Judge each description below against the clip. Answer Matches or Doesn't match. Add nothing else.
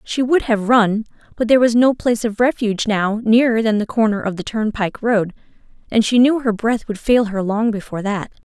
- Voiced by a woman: Matches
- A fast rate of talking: Matches